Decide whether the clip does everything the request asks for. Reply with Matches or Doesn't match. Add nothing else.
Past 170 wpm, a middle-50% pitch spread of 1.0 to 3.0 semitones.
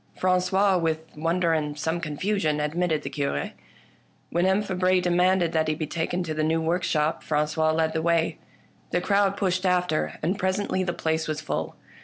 Matches